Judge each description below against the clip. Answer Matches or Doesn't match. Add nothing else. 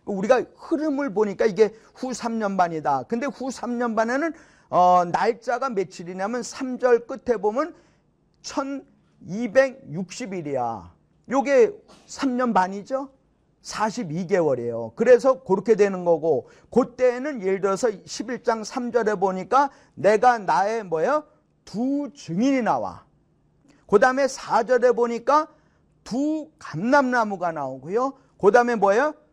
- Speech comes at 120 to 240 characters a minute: Matches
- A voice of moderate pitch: Doesn't match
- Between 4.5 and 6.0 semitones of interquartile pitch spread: Matches